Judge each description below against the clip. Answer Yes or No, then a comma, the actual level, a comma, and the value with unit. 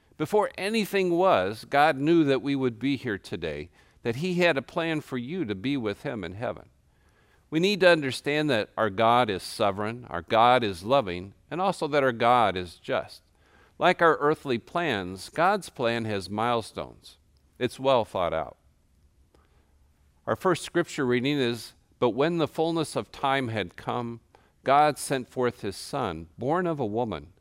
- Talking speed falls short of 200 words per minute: Yes, average, 170 wpm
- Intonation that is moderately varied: No, wide, 7.5 semitones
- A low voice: Yes, low, 125 Hz